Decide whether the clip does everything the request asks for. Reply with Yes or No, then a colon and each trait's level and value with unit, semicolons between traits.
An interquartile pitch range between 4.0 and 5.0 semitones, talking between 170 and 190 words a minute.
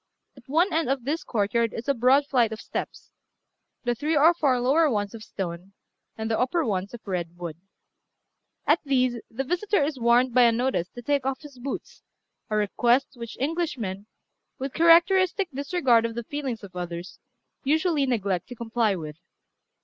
Yes: average, 4.7 semitones; average, 175 wpm